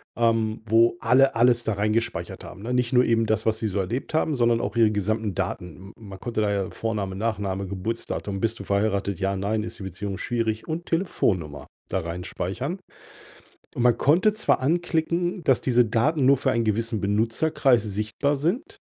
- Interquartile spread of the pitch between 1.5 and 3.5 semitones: No, average, 3.9 semitones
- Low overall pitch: Yes, low, 115 Hz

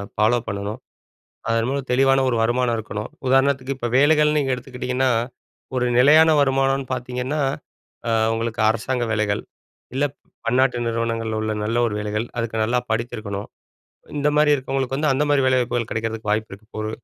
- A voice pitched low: Yes, low, 125 Hz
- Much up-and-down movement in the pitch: No, average, 3.1 semitones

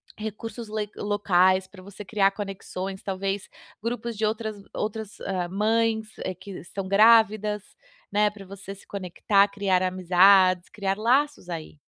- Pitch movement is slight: Yes, narrow, 2.2 semitones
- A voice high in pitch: Yes, high, 200 Hz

